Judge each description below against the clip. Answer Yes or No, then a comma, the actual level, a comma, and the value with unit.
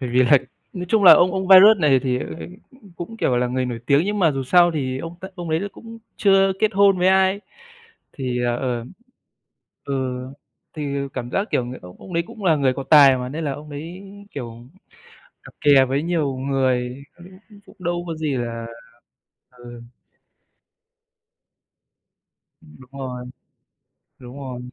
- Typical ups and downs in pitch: No, wide, 6.1 semitones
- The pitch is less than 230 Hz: Yes, medium, 140 Hz